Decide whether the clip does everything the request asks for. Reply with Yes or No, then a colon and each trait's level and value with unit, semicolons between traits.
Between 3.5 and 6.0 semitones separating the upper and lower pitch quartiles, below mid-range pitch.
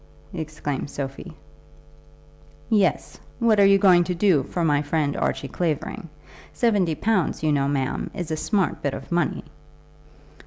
No: average, 5.1 semitones; medium, 165 Hz